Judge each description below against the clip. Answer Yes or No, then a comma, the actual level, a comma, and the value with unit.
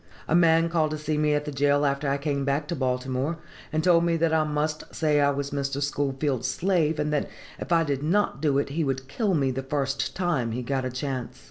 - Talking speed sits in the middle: No, fast, 240 wpm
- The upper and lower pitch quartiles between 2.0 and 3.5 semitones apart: Yes, narrow, 2.4 semitones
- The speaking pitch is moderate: Yes, medium, 145 Hz